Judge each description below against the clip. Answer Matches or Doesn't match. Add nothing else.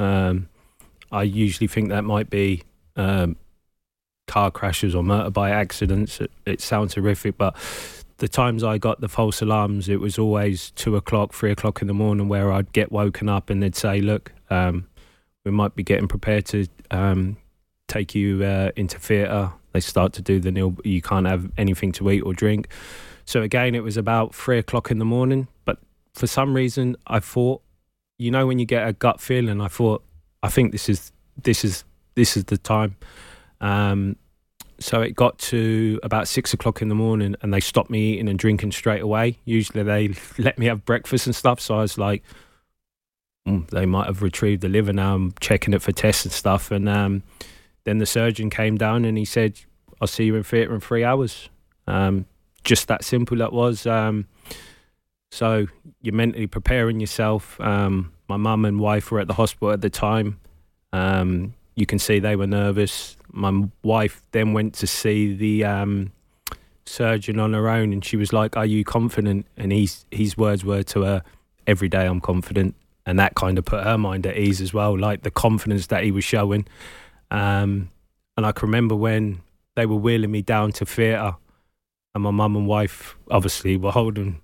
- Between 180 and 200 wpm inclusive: Matches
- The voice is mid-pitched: Doesn't match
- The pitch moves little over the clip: Matches